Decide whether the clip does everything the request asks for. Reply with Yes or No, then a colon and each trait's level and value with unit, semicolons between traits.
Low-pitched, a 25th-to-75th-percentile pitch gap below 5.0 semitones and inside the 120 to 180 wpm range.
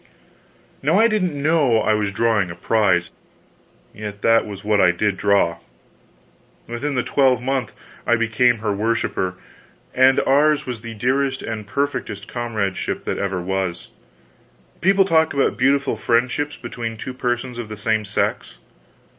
Yes: low, 115 Hz; average, 4.5 semitones; average, 145 wpm